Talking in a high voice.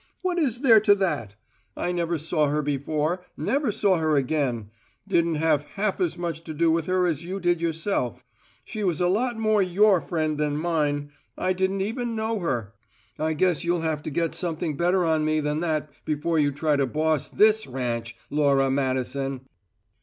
No: medium, 160 Hz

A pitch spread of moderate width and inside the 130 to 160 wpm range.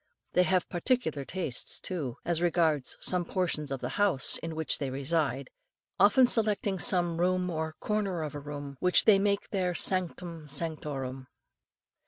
Yes: average, 3.9 semitones; average, 155 wpm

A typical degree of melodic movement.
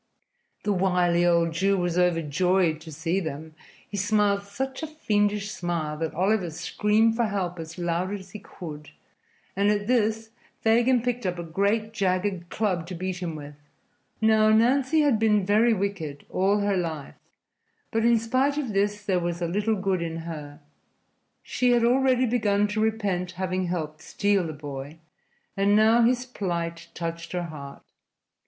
Yes: average, 4.3 semitones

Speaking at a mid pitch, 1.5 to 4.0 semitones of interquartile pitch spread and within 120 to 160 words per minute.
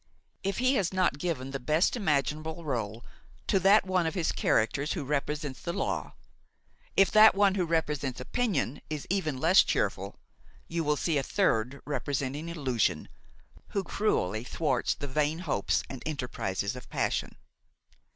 No: medium, 150 Hz; average, 5.1 semitones; average, 150 wpm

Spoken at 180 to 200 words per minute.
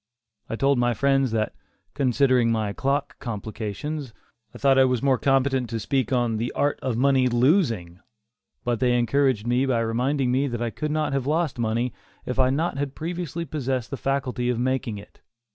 Yes: average, 185 wpm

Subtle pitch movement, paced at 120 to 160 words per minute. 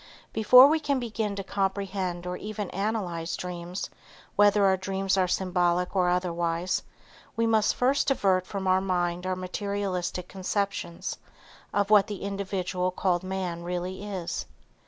Yes: narrow, 2.1 semitones; average, 140 wpm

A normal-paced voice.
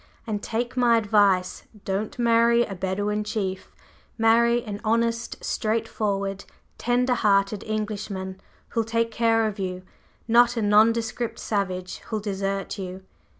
No: slow, 125 wpm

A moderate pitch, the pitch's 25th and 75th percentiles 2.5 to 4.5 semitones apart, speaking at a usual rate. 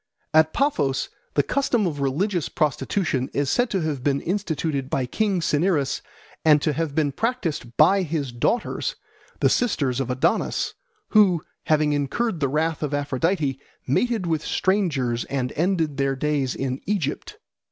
No: medium, 155 Hz; average, 5.3 semitones; average, 150 wpm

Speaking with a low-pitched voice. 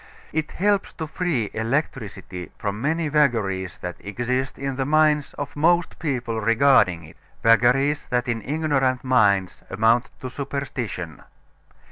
Yes: low, 130 Hz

